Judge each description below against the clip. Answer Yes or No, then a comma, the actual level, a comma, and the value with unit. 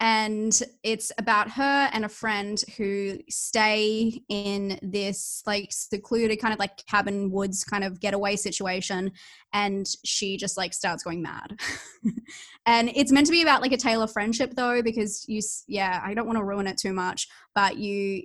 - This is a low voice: No, high, 210 Hz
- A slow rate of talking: No, average, 175 wpm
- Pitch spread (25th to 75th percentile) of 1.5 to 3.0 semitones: Yes, narrow, 2.4 semitones